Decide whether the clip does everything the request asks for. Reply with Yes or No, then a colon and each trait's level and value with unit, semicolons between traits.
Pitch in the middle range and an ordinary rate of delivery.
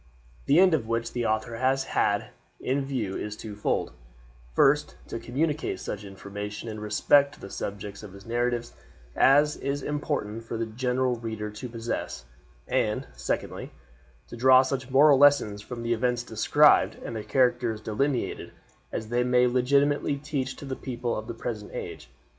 No: low, 120 Hz; average, 160 wpm